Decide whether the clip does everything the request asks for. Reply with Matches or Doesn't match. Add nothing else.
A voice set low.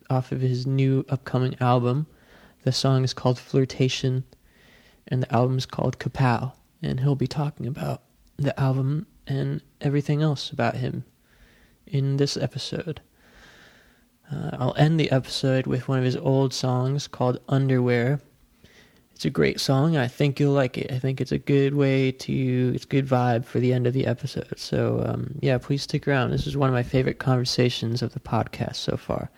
Matches